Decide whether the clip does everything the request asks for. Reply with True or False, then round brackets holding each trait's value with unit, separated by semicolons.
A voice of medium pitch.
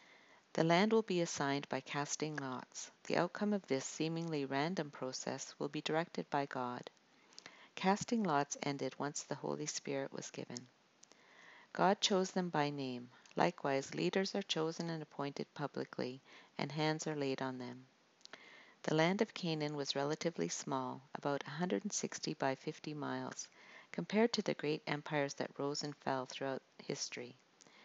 True (150 Hz)